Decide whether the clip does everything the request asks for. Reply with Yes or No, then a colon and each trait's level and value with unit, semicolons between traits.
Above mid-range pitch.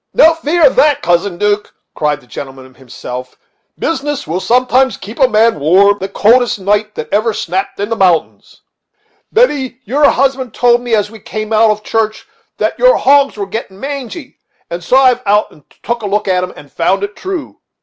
Yes: high, 215 Hz